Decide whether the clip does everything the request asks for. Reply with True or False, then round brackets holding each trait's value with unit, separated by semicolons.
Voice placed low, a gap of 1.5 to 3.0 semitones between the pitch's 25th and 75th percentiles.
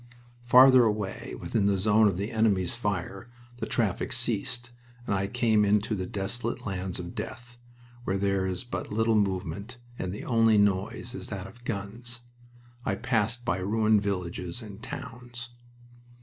False (105 Hz; 3.4 semitones)